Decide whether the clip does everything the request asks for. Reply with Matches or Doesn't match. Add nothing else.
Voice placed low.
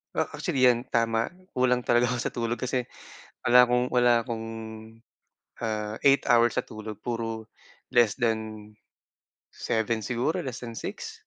Matches